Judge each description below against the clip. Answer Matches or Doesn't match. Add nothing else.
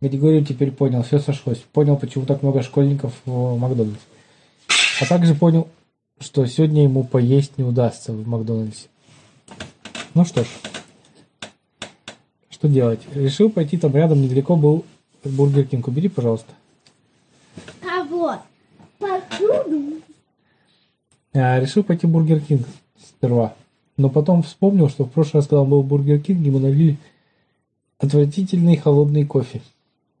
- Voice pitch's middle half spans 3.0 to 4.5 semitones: Matches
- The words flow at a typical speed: Matches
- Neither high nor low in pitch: Matches